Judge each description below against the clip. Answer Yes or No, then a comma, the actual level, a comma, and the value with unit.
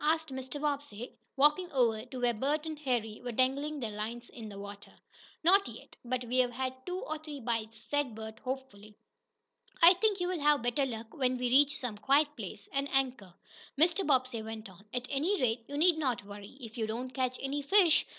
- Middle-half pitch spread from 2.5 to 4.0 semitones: No, average, 4.5 semitones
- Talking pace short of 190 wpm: No, average, 200 wpm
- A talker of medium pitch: No, very high, 255 Hz